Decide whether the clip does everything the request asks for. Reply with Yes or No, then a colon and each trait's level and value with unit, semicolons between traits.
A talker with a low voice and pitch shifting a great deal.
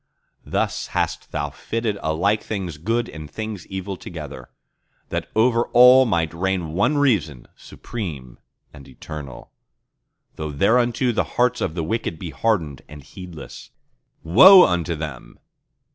Yes: very low, 90 Hz; wide, 6.6 semitones